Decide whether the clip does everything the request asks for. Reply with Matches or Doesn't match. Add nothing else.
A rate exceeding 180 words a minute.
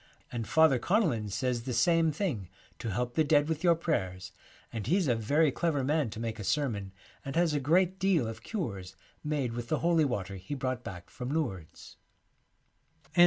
Matches